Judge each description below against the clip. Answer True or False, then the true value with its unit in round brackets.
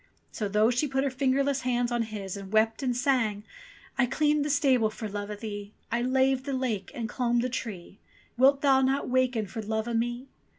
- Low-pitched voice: False (240 Hz)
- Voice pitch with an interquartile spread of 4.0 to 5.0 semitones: False (3.5 semitones)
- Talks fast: True (215 wpm)